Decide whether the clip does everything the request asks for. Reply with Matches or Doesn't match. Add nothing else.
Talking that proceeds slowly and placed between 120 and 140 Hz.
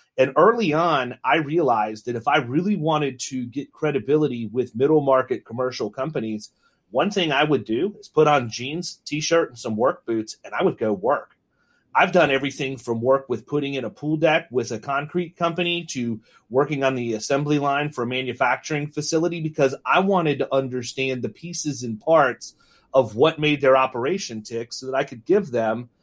Doesn't match